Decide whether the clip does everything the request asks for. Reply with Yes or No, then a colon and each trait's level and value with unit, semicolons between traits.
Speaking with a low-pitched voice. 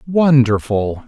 Yes: low, 125 Hz